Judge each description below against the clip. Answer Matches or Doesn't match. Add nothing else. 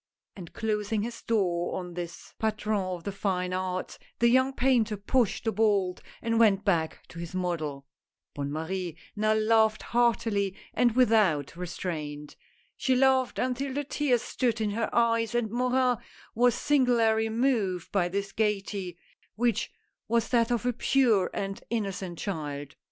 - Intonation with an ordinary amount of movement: Matches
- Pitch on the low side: Doesn't match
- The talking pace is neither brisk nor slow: Matches